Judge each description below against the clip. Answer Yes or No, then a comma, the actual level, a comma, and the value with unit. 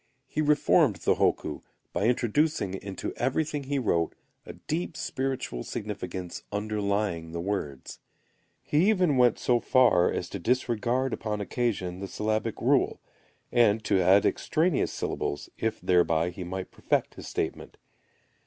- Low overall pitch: Yes, low, 110 Hz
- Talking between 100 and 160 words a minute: Yes, slow, 135 wpm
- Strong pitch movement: Yes, wide, 5.9 semitones